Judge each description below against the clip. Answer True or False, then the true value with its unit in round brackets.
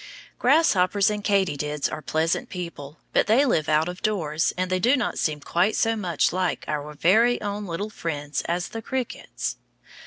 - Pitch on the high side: False (180 Hz)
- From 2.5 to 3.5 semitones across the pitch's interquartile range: False (5.4 semitones)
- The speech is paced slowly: False (175 wpm)